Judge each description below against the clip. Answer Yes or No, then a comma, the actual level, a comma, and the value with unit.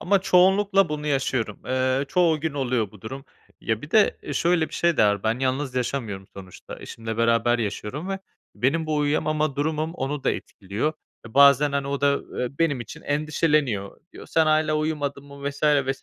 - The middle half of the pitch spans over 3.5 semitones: Yes, average, 3.9 semitones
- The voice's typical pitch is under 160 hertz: Yes, medium, 140 Hz